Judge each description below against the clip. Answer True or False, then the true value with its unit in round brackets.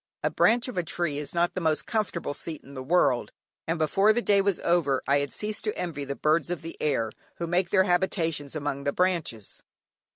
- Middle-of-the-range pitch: True (165 Hz)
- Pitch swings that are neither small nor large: True (4.2 semitones)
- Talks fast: True (220 wpm)